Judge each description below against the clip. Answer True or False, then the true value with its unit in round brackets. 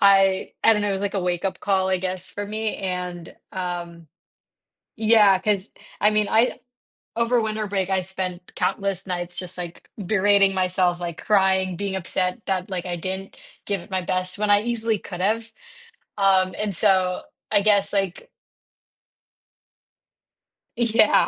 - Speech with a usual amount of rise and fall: False (2.0 semitones)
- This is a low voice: False (190 Hz)